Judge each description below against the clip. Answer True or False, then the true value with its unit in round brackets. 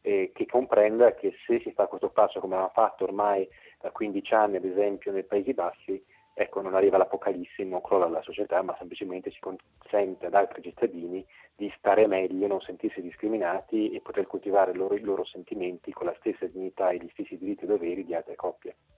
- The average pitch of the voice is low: True (105 Hz)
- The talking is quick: True (190 wpm)